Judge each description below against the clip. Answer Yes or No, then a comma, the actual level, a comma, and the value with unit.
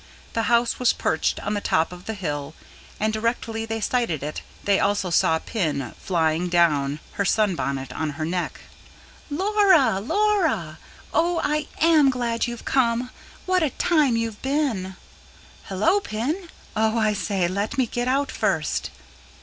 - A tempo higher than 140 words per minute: Yes, average, 150 wpm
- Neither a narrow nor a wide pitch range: No, wide, 7.1 semitones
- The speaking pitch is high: Yes, high, 220 Hz